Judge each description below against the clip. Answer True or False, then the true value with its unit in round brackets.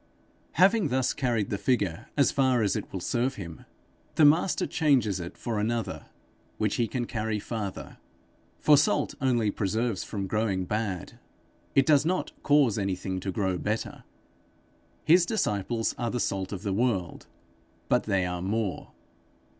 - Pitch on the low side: True (110 Hz)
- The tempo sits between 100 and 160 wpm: True (155 wpm)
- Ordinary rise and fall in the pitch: True (4.9 semitones)